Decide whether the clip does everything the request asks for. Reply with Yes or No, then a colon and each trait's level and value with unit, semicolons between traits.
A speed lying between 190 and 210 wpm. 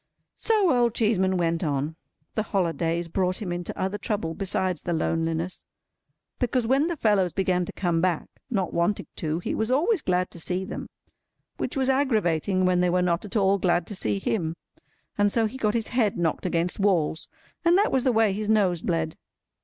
Yes: average, 195 wpm